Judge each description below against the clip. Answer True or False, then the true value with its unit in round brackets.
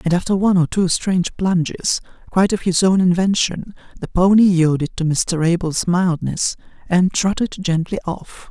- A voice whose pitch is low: False (180 Hz)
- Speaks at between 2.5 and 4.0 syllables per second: False (4.9 syllables/s)